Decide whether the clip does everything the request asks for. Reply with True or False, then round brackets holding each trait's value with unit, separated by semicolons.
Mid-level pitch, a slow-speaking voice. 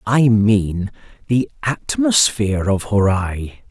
False (110 Hz; 95 wpm)